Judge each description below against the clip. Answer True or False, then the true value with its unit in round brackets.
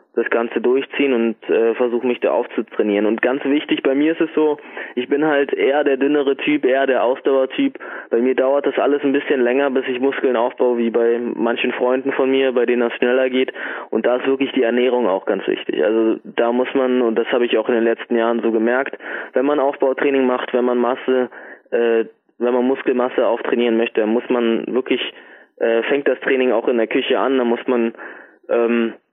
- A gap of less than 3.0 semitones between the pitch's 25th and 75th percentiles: True (2.5 semitones)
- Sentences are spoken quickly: True (215 wpm)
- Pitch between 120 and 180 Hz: True (125 Hz)